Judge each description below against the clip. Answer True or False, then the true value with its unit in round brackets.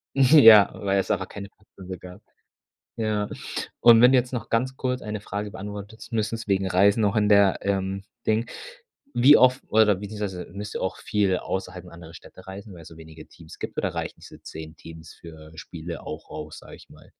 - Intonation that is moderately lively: True (3.2 semitones)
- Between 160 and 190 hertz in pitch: False (100 Hz)